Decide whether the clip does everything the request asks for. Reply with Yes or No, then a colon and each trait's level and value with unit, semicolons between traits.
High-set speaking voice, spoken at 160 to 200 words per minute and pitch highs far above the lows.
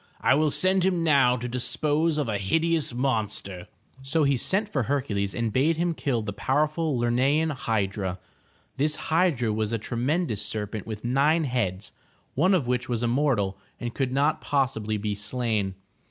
No: low, 125 Hz; average, 170 wpm; wide, 5.8 semitones